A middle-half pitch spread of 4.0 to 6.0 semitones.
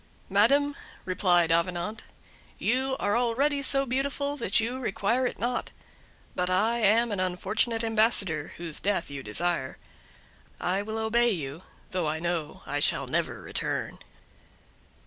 Yes: wide, 5.4 semitones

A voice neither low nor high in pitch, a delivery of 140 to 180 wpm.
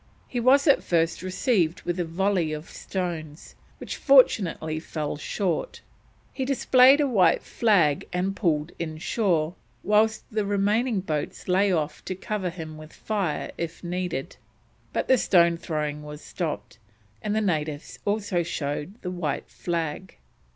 Yes: medium, 180 Hz; average, 145 wpm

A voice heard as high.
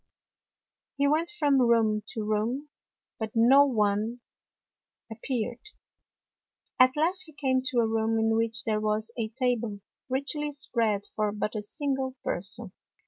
Yes: high, 235 Hz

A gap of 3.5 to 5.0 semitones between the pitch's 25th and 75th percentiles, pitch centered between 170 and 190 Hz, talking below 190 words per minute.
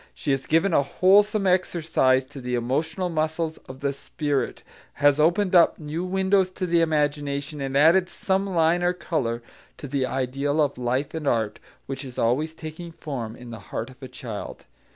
No: average, 4.5 semitones; medium, 150 Hz; average, 180 wpm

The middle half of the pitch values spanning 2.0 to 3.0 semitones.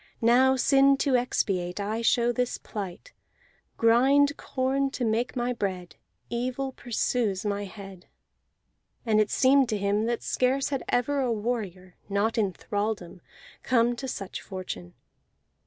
No: average, 4.2 semitones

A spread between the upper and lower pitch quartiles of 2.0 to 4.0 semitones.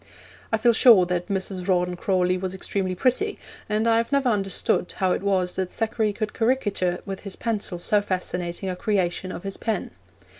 Yes: average, 3.3 semitones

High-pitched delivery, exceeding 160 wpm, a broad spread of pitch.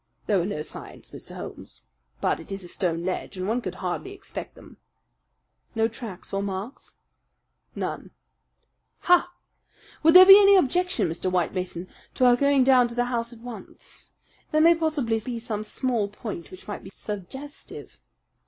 Yes: high, 230 Hz; average, 170 wpm; wide, 6.7 semitones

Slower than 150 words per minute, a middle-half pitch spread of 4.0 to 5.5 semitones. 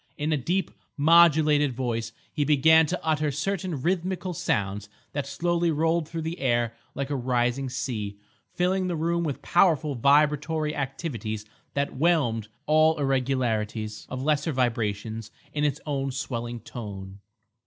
Yes: average, 140 wpm; average, 5.0 semitones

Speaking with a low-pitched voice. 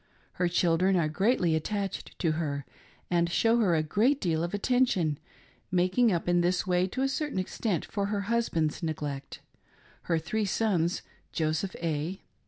No: medium, 180 Hz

